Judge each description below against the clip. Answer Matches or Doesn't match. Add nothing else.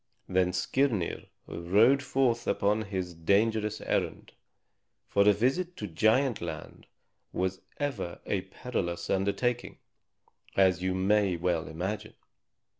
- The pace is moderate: Doesn't match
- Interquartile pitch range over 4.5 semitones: Doesn't match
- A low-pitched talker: Matches